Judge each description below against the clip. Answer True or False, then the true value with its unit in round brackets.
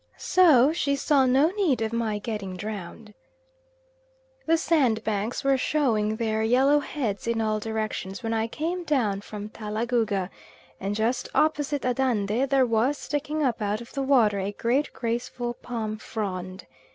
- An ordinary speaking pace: True (150 wpm)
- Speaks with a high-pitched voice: True (230 Hz)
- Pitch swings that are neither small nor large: True (4.4 semitones)